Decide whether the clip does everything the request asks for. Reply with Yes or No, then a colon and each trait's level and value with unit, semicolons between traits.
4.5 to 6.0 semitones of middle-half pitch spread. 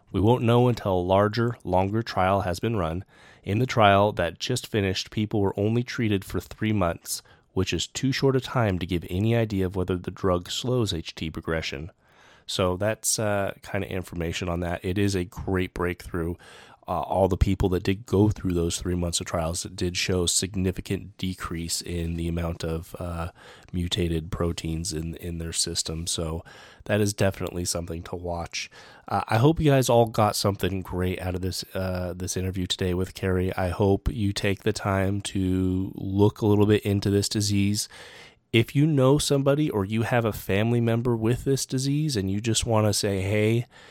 No: average, 3.4 semitones